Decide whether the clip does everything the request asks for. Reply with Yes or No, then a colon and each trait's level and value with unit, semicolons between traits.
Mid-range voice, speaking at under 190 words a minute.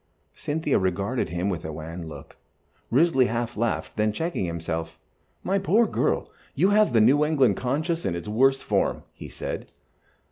No: low, 120 Hz; average, 165 wpm